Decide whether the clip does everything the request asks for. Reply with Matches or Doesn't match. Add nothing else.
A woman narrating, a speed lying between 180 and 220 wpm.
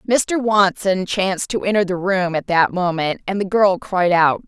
Matches